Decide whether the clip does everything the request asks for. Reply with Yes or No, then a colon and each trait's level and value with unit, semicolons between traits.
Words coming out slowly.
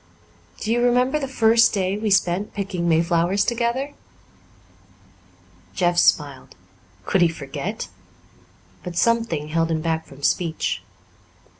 Yes: slow, 120 wpm